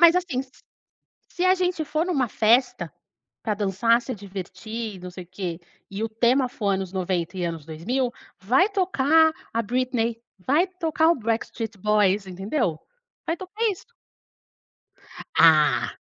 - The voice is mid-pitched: No, high, 230 Hz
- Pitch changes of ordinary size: No, wide, 8.4 semitones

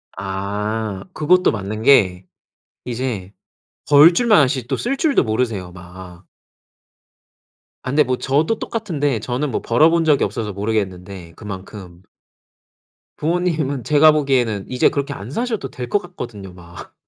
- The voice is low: Yes, low, 120 Hz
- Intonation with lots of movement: Yes, wide, 7.2 semitones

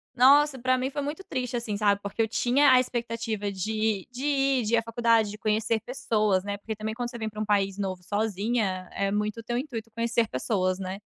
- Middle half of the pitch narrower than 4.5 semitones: Yes, average, 3.0 semitones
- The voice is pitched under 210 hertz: No, high, 220 Hz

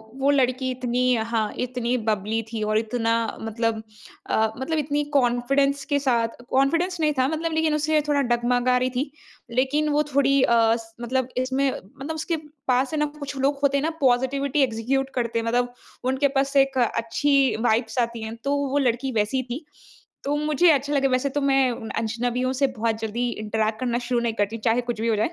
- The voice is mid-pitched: No, very high, 255 Hz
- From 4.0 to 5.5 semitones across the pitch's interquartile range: No, average, 3.3 semitones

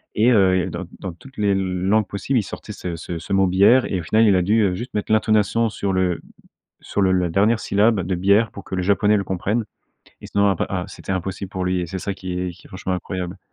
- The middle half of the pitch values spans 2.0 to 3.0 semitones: Yes, narrow, 2.4 semitones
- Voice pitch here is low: Yes, very low, 95 Hz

